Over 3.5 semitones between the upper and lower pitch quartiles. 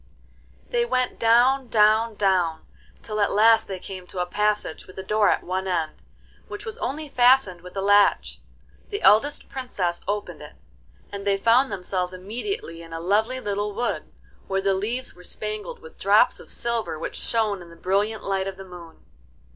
Yes: average, 4.0 semitones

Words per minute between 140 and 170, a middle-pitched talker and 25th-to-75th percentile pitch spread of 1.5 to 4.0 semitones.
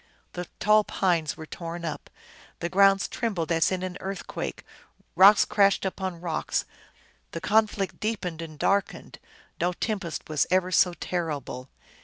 Yes: average, 145 wpm; medium, 180 Hz; average, 3.0 semitones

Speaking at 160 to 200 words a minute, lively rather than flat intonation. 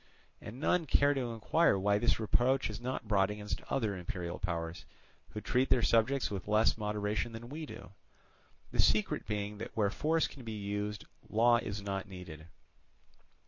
No: average, 170 wpm; average, 3.2 semitones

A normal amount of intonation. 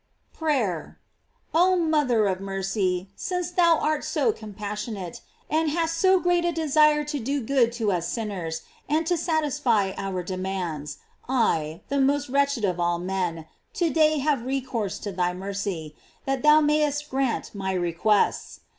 No: wide, 8.0 semitones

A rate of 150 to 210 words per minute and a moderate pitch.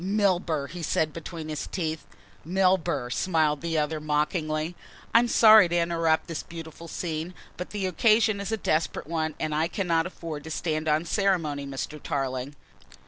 Yes: average, 165 wpm; medium, 165 Hz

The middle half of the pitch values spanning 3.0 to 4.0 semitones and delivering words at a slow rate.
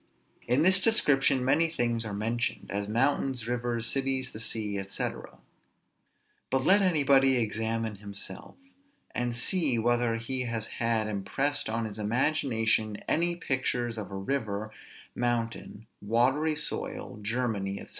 Yes: average, 3.6 semitones; slow, 130 wpm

